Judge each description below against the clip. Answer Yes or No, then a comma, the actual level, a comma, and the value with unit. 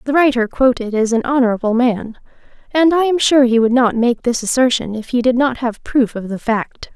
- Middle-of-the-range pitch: No, high, 245 Hz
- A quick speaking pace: Yes, fast, 225 wpm